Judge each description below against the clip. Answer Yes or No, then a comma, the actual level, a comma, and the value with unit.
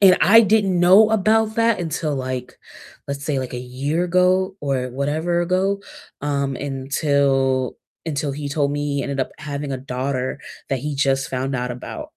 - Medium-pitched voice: Yes, medium, 145 Hz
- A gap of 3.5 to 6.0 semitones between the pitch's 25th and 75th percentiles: Yes, average, 5.2 semitones